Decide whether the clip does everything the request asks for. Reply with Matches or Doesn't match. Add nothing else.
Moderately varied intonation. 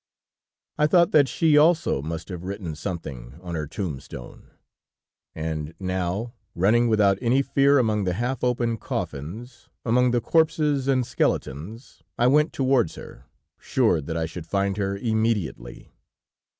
Doesn't match